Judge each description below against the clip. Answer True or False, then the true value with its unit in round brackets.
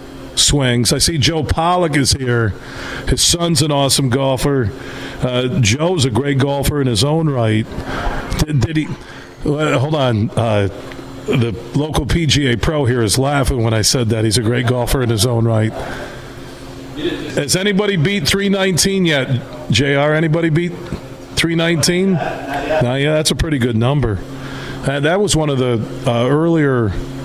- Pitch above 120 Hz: True (140 Hz)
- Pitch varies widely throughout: False (4.3 semitones)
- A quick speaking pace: False (160 wpm)